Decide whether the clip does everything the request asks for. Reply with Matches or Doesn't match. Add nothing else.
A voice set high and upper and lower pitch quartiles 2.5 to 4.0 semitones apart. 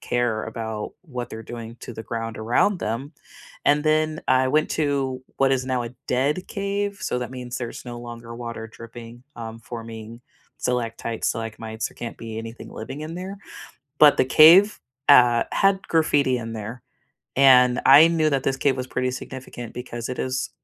Doesn't match